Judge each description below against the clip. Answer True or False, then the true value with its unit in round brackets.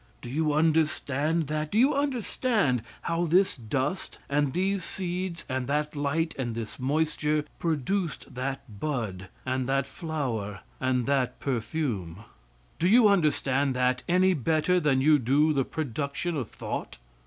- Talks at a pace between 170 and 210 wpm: False (145 wpm)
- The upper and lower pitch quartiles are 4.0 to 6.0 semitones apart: True (4.5 semitones)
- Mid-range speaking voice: True (150 Hz)